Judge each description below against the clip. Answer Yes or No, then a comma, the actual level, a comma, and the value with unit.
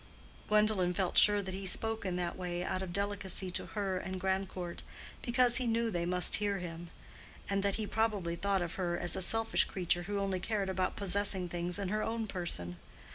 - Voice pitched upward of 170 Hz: Yes, high, 190 Hz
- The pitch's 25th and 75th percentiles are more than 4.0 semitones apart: No, narrow, 2.5 semitones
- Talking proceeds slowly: No, average, 195 wpm